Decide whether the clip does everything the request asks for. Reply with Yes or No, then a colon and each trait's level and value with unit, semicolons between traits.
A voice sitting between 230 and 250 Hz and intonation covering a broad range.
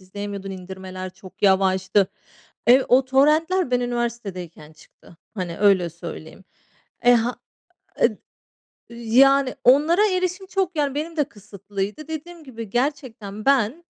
Yes: high, 235 Hz; wide, 6.8 semitones